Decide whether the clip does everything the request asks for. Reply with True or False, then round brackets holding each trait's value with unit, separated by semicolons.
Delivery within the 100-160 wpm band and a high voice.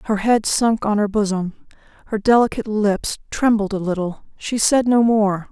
False (175 wpm; 210 Hz)